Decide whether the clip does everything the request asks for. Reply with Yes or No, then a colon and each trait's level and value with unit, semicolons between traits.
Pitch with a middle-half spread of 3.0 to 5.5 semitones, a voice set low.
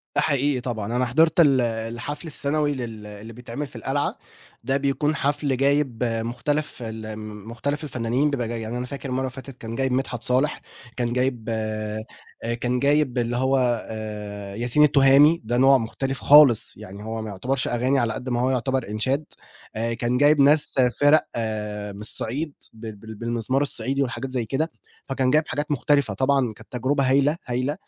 Yes: average, 3.6 semitones; low, 125 Hz